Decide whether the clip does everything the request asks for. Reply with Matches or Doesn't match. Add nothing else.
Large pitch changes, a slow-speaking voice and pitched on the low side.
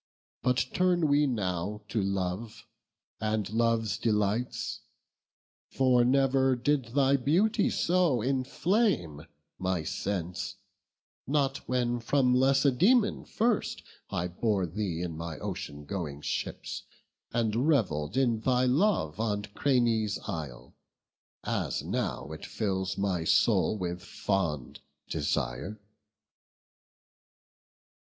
Matches